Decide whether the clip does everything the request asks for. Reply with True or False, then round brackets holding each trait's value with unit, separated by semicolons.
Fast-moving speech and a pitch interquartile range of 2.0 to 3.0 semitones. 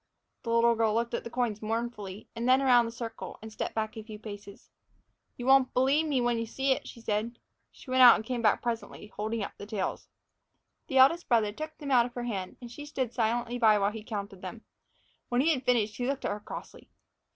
True (230 wpm; 2.7 semitones)